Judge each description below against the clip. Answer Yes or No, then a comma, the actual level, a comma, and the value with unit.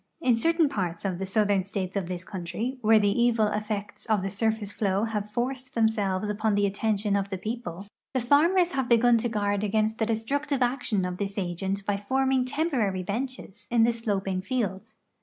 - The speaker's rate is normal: Yes, average, 190 wpm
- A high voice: Yes, high, 215 Hz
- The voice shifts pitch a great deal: No, average, 3.4 semitones